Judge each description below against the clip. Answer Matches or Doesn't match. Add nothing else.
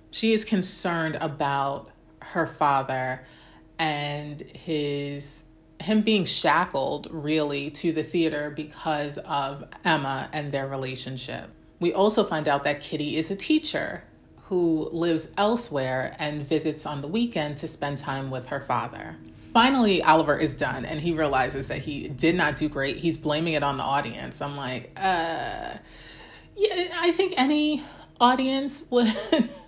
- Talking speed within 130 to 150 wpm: Matches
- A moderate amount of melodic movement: Matches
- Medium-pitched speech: Matches